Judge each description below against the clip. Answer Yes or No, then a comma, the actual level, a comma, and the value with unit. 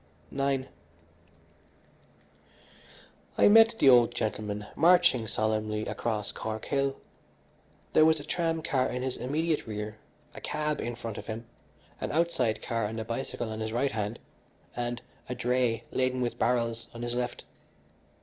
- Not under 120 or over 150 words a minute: Yes, average, 145 wpm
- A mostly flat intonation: No, average, 3.8 semitones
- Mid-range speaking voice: No, low, 120 Hz